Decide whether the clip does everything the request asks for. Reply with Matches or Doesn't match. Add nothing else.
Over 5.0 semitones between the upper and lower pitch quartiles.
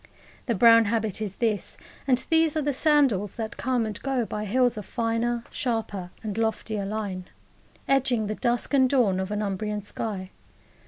Doesn't match